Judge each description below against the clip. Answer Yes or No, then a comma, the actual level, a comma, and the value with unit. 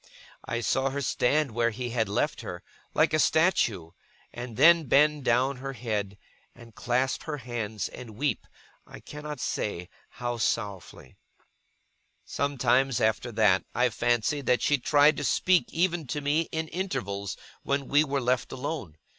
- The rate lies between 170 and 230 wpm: No, average, 155 wpm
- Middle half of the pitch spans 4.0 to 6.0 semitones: Yes, average, 4.4 semitones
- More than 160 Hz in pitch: No, low, 125 Hz